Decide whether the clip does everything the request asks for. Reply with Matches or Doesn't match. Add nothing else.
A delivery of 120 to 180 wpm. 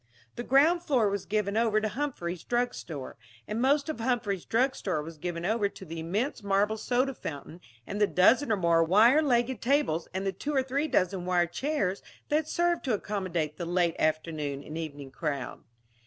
Doesn't match